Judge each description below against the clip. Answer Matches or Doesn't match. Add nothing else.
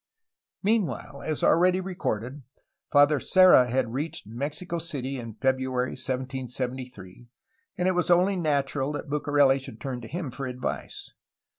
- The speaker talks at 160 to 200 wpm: Doesn't match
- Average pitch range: Matches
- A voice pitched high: Doesn't match